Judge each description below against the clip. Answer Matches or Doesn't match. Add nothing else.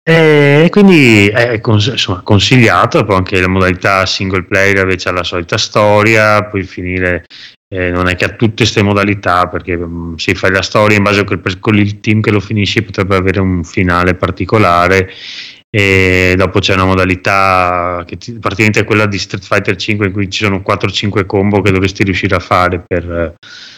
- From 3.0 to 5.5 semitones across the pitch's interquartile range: Doesn't match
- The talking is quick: Matches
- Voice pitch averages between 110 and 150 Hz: Doesn't match